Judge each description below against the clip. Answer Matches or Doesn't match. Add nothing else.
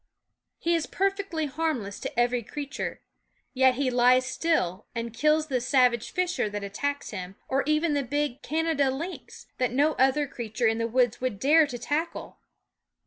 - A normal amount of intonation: Matches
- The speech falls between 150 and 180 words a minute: Matches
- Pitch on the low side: Doesn't match